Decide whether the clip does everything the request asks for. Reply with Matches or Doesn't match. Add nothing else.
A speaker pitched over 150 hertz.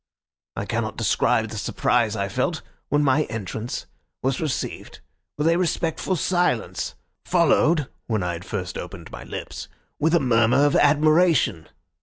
Doesn't match